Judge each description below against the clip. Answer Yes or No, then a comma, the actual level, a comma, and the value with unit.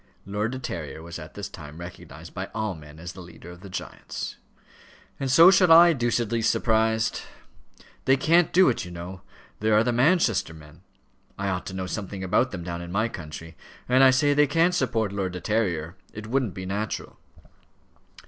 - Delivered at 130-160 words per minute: No, average, 190 wpm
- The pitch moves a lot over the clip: Yes, wide, 6.4 semitones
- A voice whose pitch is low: Yes, low, 105 Hz